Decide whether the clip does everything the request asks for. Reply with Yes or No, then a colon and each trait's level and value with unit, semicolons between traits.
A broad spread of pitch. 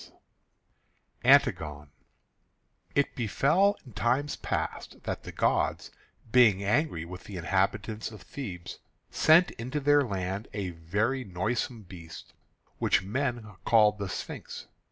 Yes: wide, 5.7 semitones